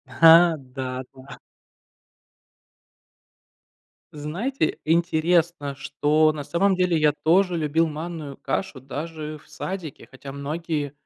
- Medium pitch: Yes, medium, 155 Hz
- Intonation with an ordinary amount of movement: Yes, average, 3.2 semitones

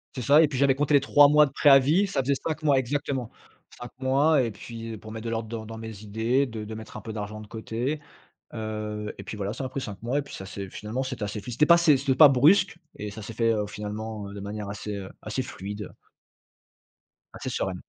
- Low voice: Yes, low, 115 Hz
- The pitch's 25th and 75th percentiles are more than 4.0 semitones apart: Yes, average, 4.5 semitones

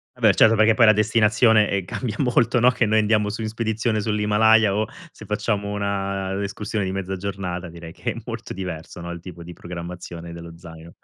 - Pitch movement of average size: Yes, average, 3.5 semitones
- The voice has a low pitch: Yes, low, 100 Hz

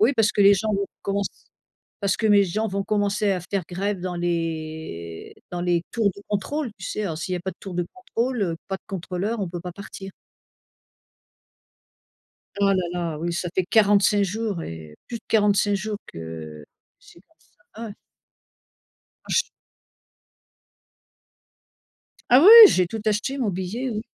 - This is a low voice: No, high, 195 Hz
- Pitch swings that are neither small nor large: Yes, average, 3.3 semitones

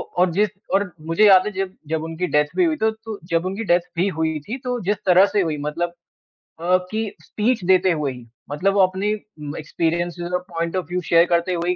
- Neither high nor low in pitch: Yes, medium, 180 Hz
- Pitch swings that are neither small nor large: Yes, average, 3.2 semitones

